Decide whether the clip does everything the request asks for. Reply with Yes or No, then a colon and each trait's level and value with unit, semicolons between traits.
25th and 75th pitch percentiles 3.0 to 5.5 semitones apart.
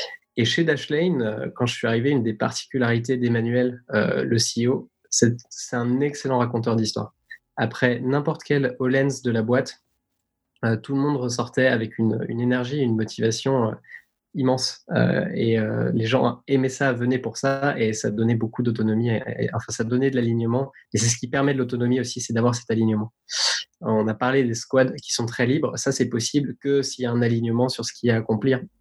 No: narrow, 2.6 semitones